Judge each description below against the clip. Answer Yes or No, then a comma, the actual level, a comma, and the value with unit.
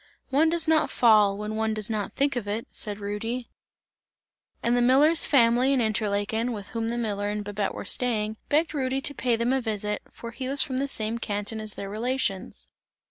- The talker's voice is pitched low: No, high, 230 Hz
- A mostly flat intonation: No, average, 3.6 semitones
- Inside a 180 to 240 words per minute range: Yes, average, 200 wpm